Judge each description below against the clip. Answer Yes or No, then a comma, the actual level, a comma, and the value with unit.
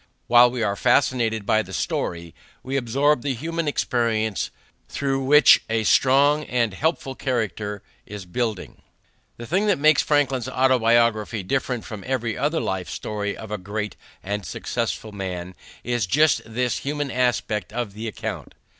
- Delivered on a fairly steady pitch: No, average, 4.3 semitones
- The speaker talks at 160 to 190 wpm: No, average, 150 wpm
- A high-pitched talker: No, low, 120 Hz